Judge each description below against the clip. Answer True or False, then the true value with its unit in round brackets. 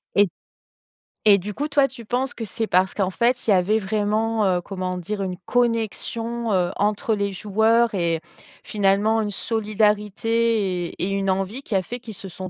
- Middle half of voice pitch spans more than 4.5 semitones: False (2.9 semitones)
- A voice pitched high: True (210 Hz)